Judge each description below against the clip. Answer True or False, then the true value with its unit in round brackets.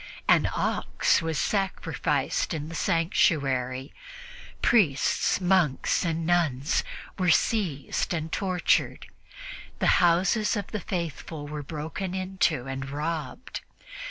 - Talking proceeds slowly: True (105 wpm)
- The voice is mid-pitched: True (165 Hz)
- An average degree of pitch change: True (4.1 semitones)